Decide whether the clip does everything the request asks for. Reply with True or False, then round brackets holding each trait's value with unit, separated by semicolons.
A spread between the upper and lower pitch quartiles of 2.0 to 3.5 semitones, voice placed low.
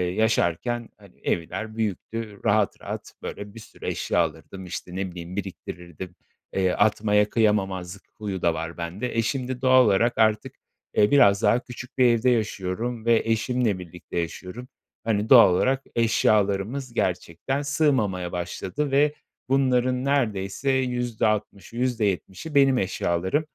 False (4.7 semitones; 110 Hz)